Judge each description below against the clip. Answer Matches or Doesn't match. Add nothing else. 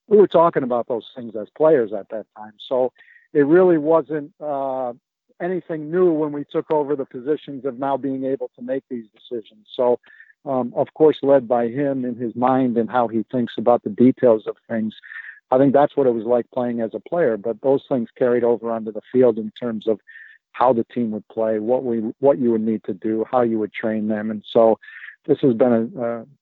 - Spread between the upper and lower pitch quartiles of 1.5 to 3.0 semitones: Doesn't match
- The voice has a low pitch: Matches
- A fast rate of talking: Matches